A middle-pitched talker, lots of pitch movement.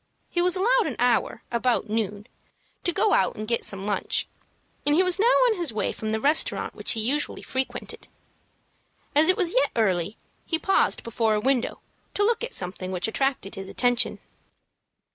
No: very high, 250 Hz; wide, 8.4 semitones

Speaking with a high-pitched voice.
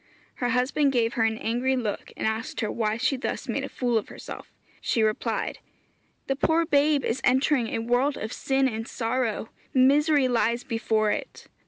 Yes: high, 245 Hz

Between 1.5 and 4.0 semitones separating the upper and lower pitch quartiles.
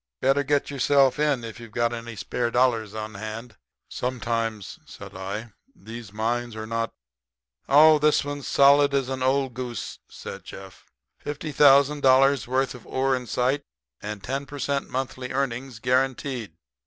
Yes: average, 3.2 semitones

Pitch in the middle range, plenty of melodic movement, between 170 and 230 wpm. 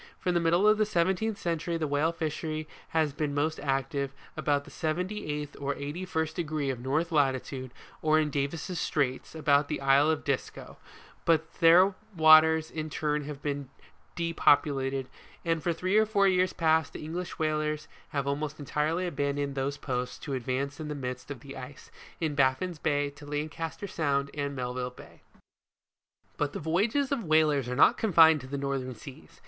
No: medium, 150 Hz; average, 2.7 semitones; average, 175 wpm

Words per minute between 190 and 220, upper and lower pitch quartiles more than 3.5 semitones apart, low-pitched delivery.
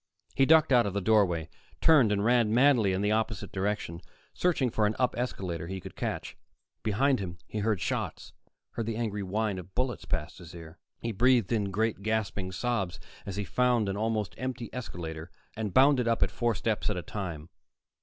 Yes: average, 195 wpm; average, 4.0 semitones; low, 105 Hz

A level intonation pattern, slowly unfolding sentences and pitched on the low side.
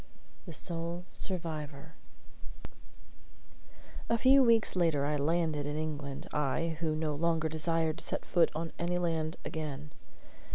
No: narrow, 2.2 semitones; slow, 130 wpm; medium, 160 Hz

